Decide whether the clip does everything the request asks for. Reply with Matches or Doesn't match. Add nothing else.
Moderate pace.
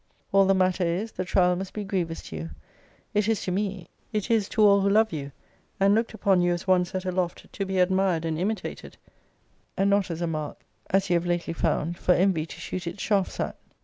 Doesn't match